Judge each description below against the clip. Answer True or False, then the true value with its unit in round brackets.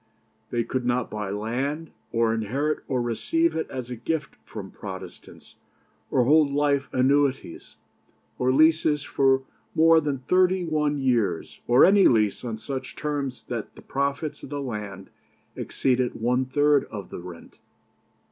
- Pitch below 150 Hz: True (135 Hz)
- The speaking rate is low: False (145 wpm)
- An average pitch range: True (3.8 semitones)